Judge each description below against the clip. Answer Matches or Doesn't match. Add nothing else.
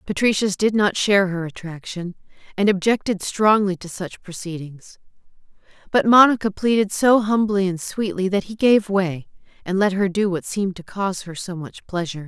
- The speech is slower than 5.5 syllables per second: Matches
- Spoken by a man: Doesn't match